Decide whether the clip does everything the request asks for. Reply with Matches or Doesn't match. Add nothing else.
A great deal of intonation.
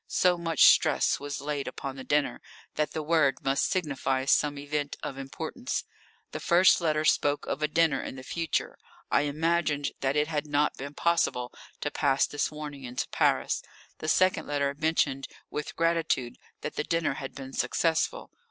Doesn't match